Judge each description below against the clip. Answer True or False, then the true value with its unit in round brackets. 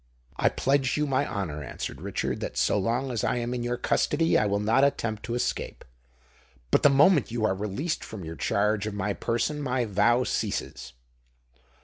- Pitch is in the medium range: False (120 Hz)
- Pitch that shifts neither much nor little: True (4.5 semitones)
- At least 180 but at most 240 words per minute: True (190 wpm)